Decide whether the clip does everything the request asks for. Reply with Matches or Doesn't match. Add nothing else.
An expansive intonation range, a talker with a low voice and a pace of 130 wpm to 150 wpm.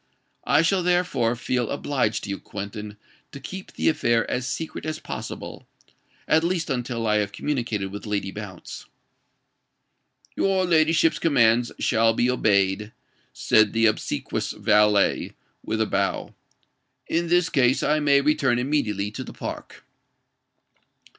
Matches